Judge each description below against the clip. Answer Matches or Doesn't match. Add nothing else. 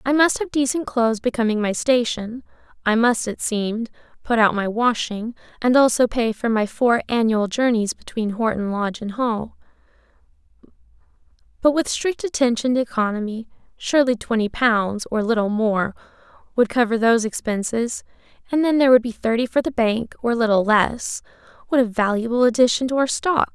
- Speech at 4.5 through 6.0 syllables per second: Matches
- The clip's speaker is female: Matches